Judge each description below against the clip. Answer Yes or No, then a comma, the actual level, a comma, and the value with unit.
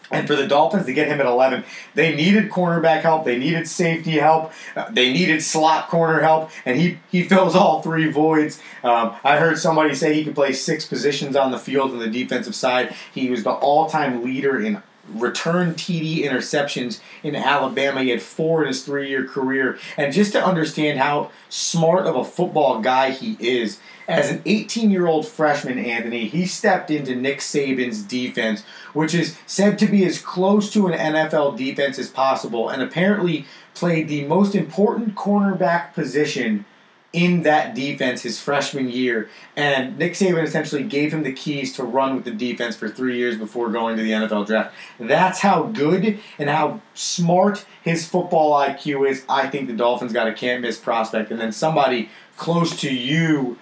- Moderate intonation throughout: Yes, average, 4.8 semitones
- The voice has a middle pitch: Yes, medium, 155 Hz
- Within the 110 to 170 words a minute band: No, average, 180 wpm